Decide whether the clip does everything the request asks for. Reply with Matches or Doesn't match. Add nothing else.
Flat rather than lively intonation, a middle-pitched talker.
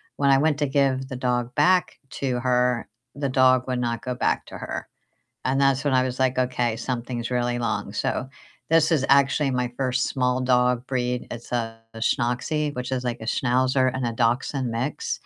Doesn't match